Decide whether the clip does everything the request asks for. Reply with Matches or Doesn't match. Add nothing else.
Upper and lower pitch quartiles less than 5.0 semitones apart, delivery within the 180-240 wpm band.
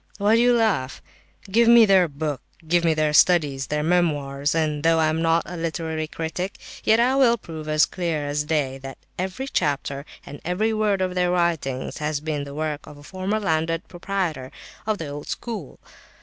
Matches